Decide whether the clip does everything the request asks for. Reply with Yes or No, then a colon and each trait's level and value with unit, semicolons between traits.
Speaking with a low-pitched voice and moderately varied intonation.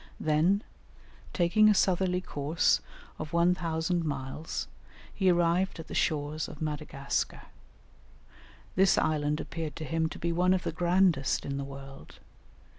No: medium, 165 Hz; average, 3.1 semitones